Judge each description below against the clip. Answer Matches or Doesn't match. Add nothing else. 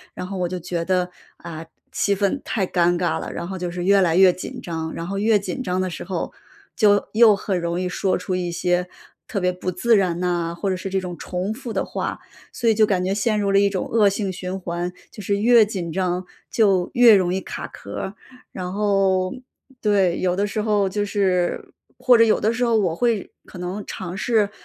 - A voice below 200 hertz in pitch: Matches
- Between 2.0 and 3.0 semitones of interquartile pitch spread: Matches